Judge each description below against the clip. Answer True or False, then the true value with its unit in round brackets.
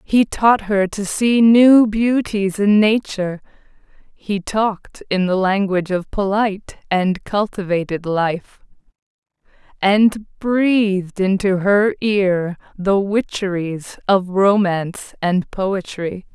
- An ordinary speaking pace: False (110 wpm)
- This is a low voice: False (200 Hz)